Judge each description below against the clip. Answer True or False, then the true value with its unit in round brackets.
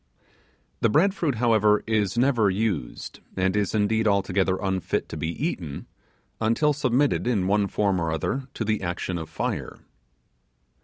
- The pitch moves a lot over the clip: False (4.1 semitones)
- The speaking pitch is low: True (105 Hz)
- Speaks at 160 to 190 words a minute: False (150 wpm)